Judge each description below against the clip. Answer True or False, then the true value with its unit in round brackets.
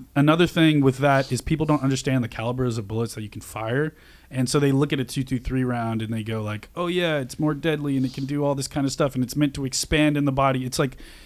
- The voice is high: False (135 Hz)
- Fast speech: True (275 wpm)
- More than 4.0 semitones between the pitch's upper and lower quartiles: False (3.0 semitones)